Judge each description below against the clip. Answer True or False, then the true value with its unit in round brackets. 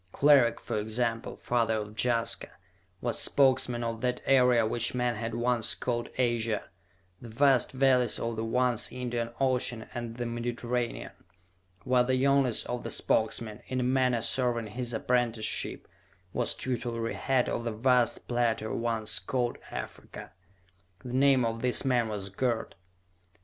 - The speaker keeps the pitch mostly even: True (1.7 semitones)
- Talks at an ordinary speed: True (145 wpm)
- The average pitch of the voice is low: True (120 Hz)